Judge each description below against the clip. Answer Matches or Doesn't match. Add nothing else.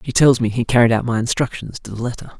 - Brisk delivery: Matches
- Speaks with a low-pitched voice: Matches